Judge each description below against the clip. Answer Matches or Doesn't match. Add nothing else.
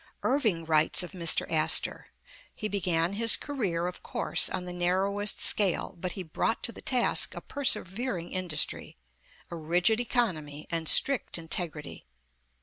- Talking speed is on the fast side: Doesn't match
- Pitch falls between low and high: Matches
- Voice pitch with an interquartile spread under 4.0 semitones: Doesn't match